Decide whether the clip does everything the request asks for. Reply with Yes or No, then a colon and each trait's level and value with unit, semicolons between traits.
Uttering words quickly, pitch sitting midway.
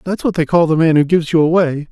Yes: fast, 315 wpm; medium, 165 Hz